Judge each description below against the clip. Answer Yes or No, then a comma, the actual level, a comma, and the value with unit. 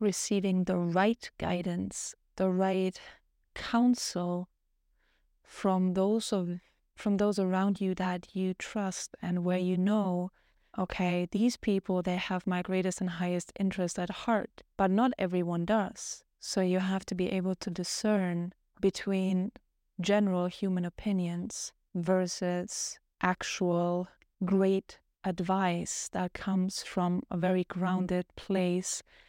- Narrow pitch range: Yes, narrow, 1.5 semitones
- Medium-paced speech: No, slow, 125 wpm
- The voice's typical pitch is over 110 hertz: Yes, medium, 185 Hz